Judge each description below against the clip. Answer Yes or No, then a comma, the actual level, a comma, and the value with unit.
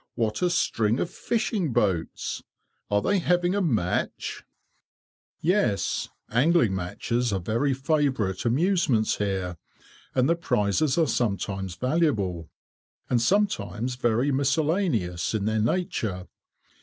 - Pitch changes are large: Yes, wide, 8.2 semitones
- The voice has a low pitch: Yes, low, 120 Hz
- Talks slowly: Yes, slow, 115 wpm